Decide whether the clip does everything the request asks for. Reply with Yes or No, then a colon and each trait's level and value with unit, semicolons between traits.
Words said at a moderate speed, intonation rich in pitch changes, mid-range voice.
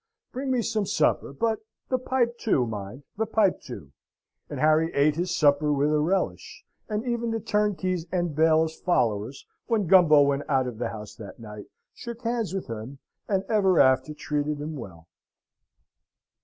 Yes: average, 170 wpm; wide, 7.4 semitones; medium, 160 Hz